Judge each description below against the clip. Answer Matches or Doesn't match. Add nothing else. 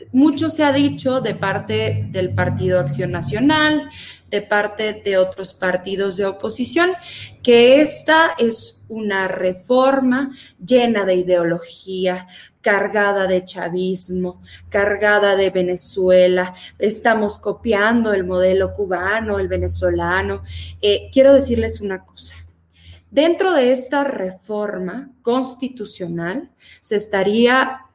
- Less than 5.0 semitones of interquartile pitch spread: Doesn't match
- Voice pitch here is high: Matches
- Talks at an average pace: Doesn't match